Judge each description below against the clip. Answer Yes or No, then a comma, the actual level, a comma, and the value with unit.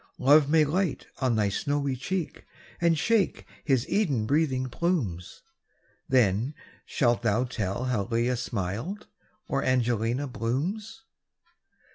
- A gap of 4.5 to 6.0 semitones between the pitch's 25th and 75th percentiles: Yes, average, 5.2 semitones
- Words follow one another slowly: Yes, slow, 115 wpm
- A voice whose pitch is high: No, low, 130 Hz